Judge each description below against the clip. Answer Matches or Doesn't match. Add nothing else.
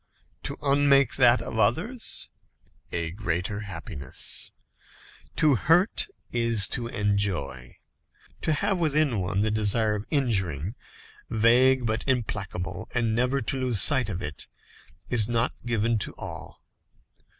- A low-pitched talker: Matches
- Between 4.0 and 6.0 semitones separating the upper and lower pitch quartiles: Matches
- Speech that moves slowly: Matches